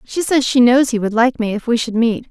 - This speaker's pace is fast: Yes, fast, 310 wpm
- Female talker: Yes, female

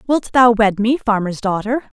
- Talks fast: No, average, 180 wpm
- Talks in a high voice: Yes, high, 225 Hz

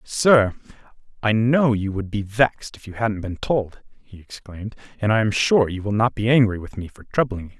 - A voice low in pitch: Yes, low, 110 Hz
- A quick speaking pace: Yes, fast, 230 wpm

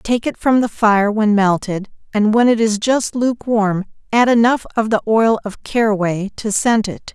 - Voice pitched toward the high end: Yes, high, 220 Hz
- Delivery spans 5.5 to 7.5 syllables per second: No, 4.6 syllables/s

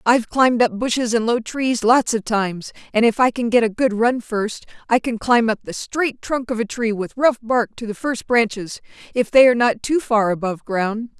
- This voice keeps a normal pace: No, fast, 230 wpm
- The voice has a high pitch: Yes, high, 230 Hz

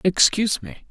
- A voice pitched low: No, high, 190 Hz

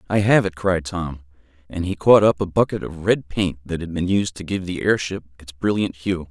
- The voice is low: Yes, very low, 90 Hz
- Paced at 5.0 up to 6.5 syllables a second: Yes, 5.2 syllables/s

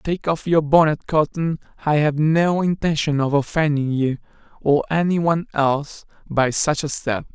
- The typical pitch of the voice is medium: Yes, medium, 150 Hz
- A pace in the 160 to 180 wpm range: Yes, average, 165 wpm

